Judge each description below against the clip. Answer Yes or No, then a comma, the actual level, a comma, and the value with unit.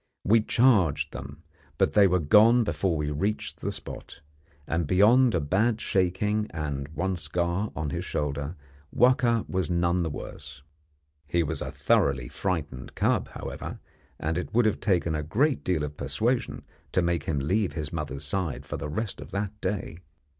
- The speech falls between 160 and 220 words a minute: Yes, average, 170 wpm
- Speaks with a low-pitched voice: Yes, very low, 85 Hz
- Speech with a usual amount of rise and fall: No, wide, 5.7 semitones